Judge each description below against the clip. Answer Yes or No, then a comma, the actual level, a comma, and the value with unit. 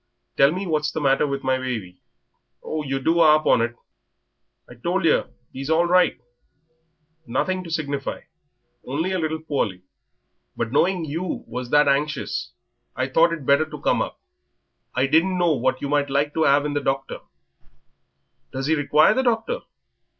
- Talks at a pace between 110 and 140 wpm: No, average, 175 wpm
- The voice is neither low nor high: Yes, medium, 150 Hz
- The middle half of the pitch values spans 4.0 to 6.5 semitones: No, average, 3.2 semitones